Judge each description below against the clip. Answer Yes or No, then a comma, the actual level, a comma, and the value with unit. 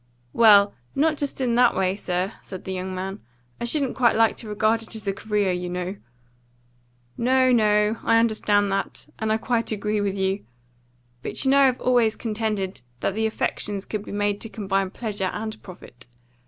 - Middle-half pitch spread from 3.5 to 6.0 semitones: No, average, 2.7 semitones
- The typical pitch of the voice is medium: No, high, 210 Hz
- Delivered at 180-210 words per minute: Yes, average, 185 wpm